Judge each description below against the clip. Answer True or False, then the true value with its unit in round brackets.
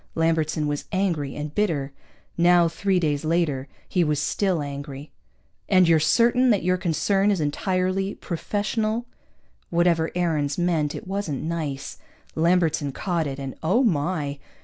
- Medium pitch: True (165 Hz)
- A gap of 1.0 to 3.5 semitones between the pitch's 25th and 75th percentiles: False (3.9 semitones)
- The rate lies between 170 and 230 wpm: False (140 wpm)